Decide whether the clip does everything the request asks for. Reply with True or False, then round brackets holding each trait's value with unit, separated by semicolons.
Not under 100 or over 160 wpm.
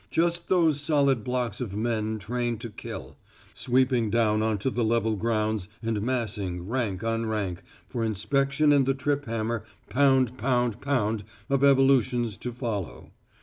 True (150 wpm)